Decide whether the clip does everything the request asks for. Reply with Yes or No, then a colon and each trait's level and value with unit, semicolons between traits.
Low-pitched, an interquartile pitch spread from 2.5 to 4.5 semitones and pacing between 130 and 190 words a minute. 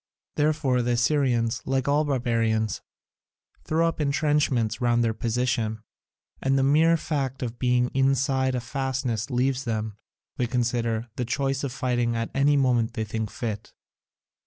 Yes: low, 125 Hz; average, 2.8 semitones; average, 145 wpm